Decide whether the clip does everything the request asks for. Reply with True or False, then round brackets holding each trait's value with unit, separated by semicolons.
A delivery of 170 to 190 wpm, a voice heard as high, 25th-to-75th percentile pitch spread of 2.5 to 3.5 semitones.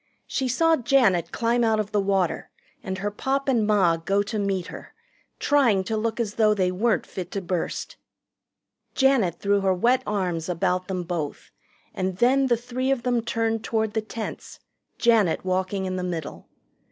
False (175 wpm; 205 Hz; 4.2 semitones)